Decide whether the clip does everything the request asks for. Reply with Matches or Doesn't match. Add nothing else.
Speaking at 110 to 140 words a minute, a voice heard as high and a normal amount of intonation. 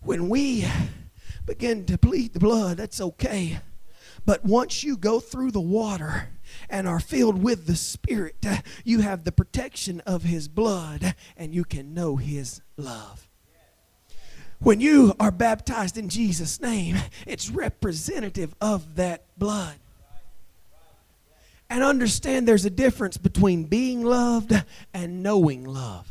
Matches